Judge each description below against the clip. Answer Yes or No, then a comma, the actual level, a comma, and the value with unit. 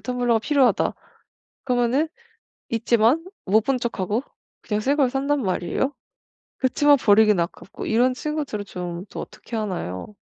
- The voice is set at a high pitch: Yes, high, 235 Hz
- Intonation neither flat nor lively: Yes, average, 4.4 semitones